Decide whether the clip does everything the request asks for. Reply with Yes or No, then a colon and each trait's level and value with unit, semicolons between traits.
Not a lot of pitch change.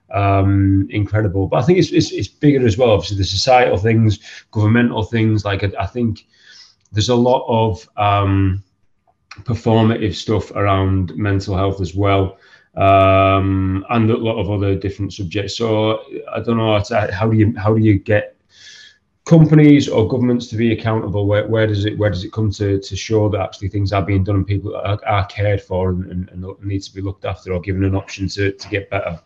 Yes: narrow, 2.3 semitones